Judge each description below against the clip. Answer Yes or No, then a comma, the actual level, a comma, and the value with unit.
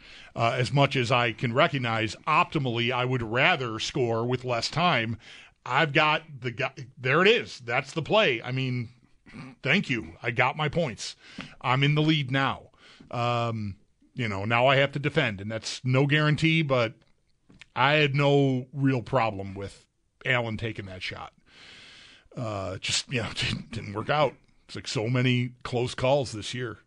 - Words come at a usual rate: Yes, average, 170 wpm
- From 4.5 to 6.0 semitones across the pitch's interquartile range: No, average, 3.4 semitones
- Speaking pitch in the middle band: No, low, 125 Hz